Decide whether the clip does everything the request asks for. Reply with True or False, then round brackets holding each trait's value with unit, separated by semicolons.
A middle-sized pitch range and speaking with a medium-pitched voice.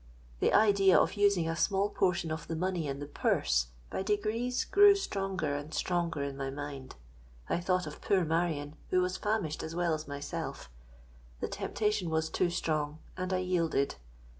True (4.8 semitones; 170 Hz)